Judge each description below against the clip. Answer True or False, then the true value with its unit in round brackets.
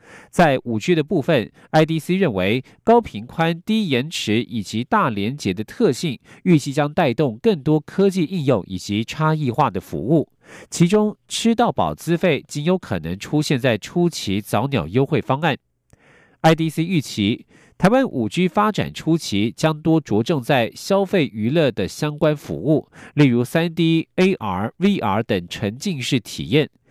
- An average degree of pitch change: False (6.4 semitones)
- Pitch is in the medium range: True (155 Hz)